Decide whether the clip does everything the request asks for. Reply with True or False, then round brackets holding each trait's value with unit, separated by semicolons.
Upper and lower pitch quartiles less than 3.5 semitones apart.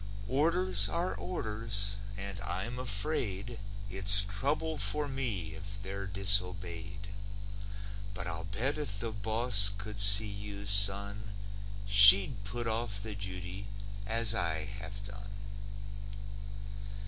True (2.4 semitones)